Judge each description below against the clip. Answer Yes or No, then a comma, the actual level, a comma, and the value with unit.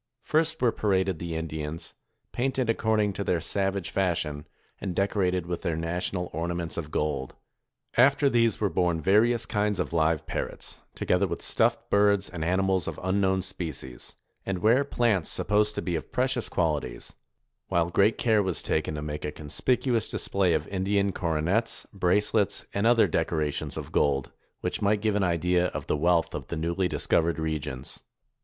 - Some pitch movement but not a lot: Yes, average, 4.1 semitones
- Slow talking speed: No, average, 170 wpm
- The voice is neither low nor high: No, very low, 90 Hz